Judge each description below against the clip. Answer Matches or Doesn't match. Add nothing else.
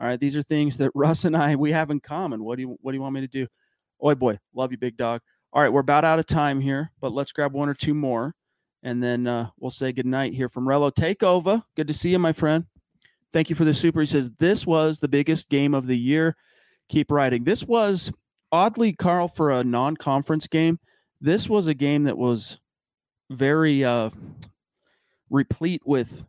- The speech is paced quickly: Matches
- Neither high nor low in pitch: Matches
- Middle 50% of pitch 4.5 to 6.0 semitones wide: Doesn't match